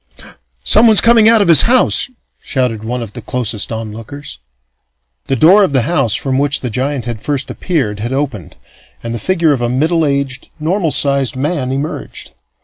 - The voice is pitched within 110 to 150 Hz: Yes, low, 135 Hz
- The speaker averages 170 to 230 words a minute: Yes, average, 175 wpm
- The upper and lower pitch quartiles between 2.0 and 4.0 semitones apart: No, average, 5.1 semitones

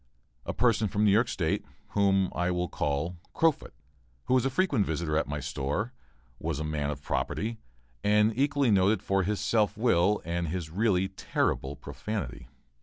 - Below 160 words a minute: No, average, 170 wpm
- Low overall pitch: Yes, very low, 95 Hz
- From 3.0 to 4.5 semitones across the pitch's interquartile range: No, average, 5.2 semitones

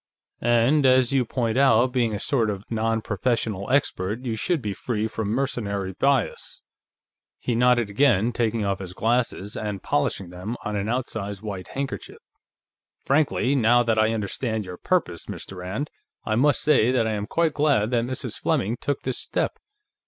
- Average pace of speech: Yes, average, 170 wpm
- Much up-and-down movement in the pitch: No, average, 3.7 semitones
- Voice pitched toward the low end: Yes, low, 115 Hz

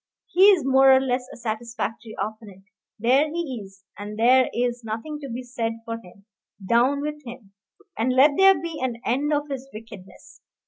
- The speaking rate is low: No, average, 180 wpm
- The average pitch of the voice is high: Yes, very high, 250 Hz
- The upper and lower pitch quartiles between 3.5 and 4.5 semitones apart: Yes, average, 3.8 semitones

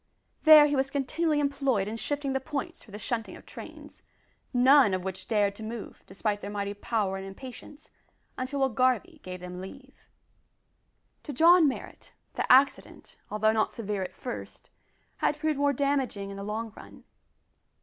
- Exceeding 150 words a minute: Yes, average, 170 wpm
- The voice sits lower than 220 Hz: No, high, 245 Hz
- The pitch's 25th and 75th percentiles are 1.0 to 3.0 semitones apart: No, wide, 5.6 semitones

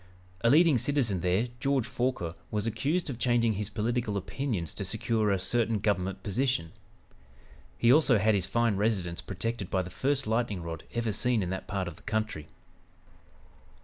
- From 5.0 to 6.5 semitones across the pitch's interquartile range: No, average, 4.0 semitones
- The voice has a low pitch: Yes, low, 110 Hz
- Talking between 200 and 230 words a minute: No, average, 170 wpm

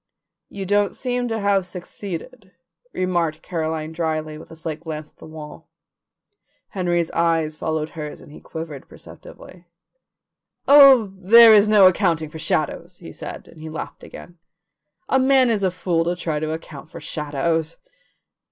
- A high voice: No, medium, 170 Hz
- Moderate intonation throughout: Yes, average, 3.9 semitones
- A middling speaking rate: Yes, average, 155 wpm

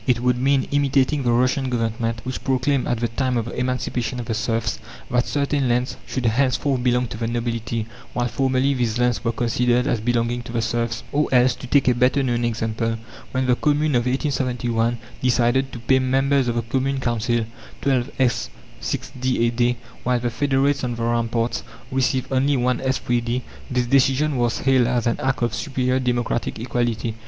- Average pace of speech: Yes, average, 185 wpm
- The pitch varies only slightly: Yes, narrow, 1.9 semitones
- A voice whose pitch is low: Yes, low, 125 Hz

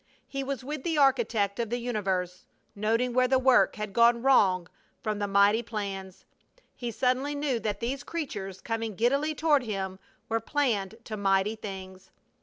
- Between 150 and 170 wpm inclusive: Yes, average, 165 wpm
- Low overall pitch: No, high, 225 Hz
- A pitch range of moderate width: Yes, average, 4.5 semitones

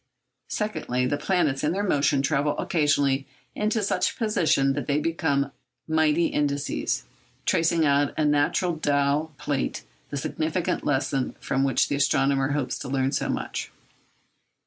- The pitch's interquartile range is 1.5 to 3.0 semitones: Yes, narrow, 2.6 semitones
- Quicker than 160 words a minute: No, average, 145 wpm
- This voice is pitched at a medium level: Yes, medium, 145 Hz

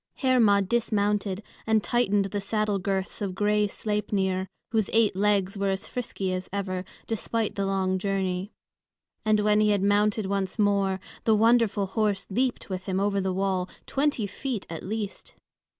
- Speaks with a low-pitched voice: No, high, 200 Hz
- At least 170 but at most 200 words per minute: No, average, 160 wpm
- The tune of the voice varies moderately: No, narrow, 1.9 semitones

